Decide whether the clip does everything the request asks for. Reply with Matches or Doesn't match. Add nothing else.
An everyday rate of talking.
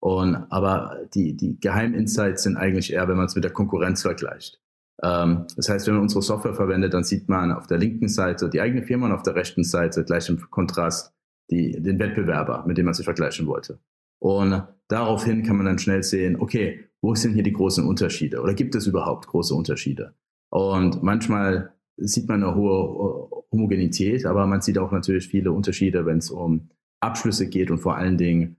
Doesn't match